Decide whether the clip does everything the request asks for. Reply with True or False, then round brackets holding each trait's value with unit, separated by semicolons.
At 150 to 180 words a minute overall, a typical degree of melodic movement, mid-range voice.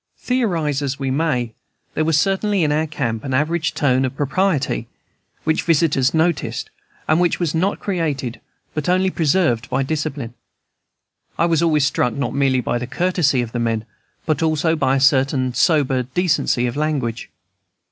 True (165 wpm; 4.0 semitones; 145 Hz)